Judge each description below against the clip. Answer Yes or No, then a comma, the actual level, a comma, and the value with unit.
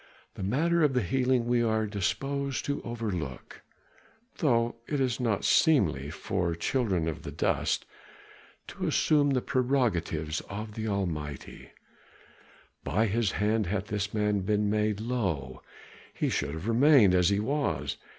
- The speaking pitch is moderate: No, low, 105 Hz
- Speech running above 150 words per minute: No, average, 140 wpm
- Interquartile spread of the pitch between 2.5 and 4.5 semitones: No, wide, 5.5 semitones